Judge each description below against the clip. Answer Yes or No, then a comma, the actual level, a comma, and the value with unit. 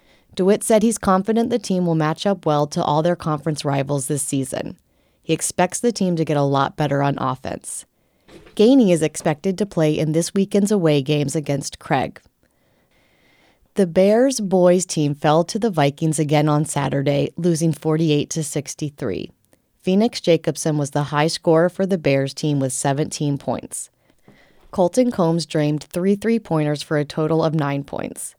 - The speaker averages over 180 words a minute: No, average, 165 wpm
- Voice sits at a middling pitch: Yes, medium, 160 Hz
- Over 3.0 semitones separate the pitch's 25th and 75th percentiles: Yes, average, 4.1 semitones